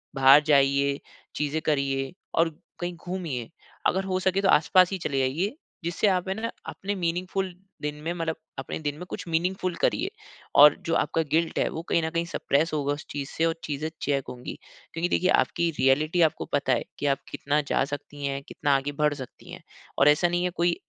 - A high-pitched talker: No, medium, 160 Hz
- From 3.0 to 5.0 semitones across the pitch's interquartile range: Yes, average, 3.8 semitones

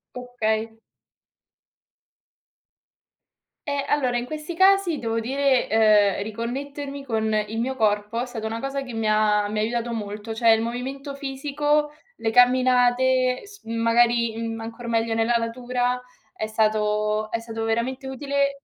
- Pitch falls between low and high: No, high, 235 Hz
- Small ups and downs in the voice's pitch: No, average, 3.0 semitones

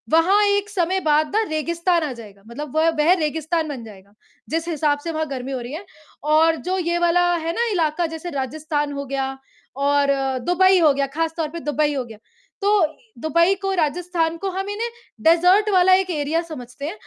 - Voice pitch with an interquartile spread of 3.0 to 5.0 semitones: Yes, average, 3.5 semitones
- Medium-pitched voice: No, very high, 320 Hz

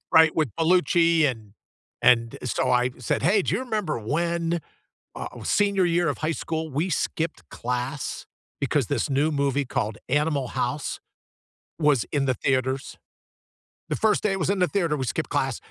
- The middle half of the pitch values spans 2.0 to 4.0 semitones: No, average, 4.7 semitones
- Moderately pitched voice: Yes, medium, 150 Hz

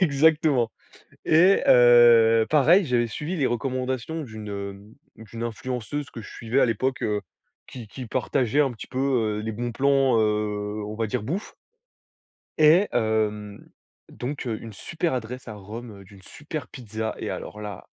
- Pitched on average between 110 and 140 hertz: Yes, low, 120 Hz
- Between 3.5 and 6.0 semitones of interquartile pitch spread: Yes, average, 4.0 semitones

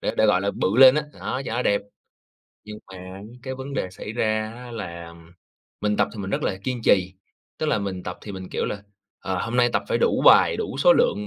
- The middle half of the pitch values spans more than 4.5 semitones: Yes, average, 5.1 semitones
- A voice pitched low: Yes, low, 105 Hz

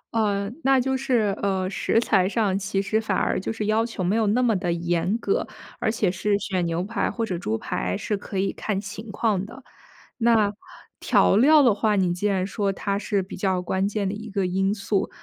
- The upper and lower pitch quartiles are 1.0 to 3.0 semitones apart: Yes, average, 2.7 semitones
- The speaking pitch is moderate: No, high, 200 Hz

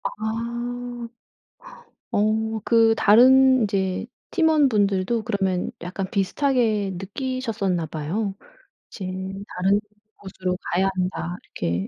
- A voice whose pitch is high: Yes, high, 205 Hz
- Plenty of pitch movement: No, average, 3.9 semitones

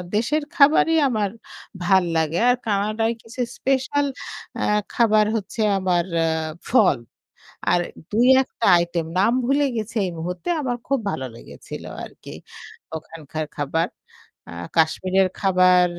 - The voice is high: Yes, high, 205 Hz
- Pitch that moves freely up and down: Yes, wide, 5.8 semitones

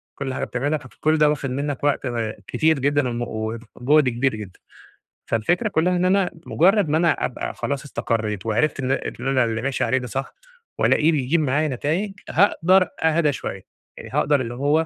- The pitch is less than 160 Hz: Yes, medium, 140 Hz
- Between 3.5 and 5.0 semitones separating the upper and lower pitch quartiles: Yes, average, 4.2 semitones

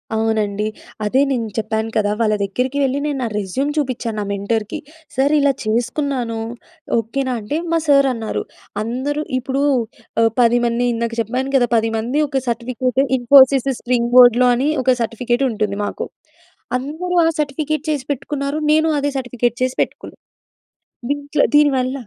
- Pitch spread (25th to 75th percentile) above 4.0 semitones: No, average, 3.4 semitones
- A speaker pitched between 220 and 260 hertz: Yes, very high, 250 Hz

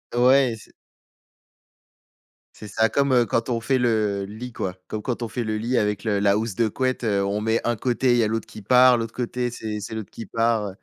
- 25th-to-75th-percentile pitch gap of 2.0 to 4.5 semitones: Yes, narrow, 2.6 semitones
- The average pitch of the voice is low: Yes, low, 115 Hz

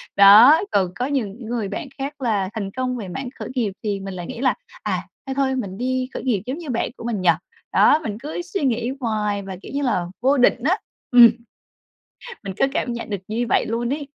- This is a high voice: Yes, high, 240 Hz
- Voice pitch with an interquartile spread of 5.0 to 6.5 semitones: No, average, 4.6 semitones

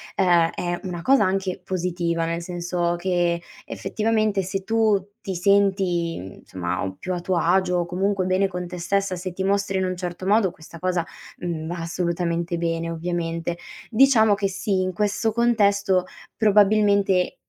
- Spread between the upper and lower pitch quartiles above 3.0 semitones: No, narrow, 2.5 semitones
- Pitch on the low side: No, medium, 185 Hz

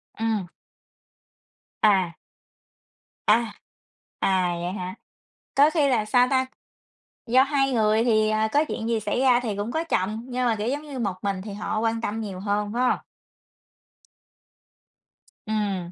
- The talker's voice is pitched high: Yes, high, 220 Hz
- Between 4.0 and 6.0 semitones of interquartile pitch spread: No, average, 3.3 semitones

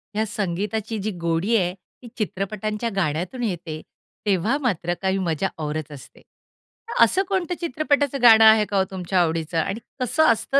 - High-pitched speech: Yes, high, 200 Hz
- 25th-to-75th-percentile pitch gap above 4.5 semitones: Yes, average, 5.1 semitones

